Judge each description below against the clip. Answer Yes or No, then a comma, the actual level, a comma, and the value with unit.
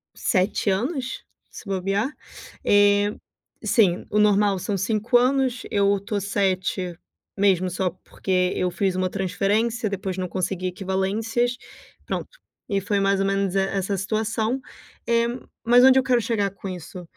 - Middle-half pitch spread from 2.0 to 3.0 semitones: Yes, average, 2.7 semitones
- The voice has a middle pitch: No, high, 200 Hz